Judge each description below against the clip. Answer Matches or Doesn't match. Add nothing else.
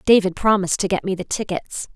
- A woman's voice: Matches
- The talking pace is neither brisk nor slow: Doesn't match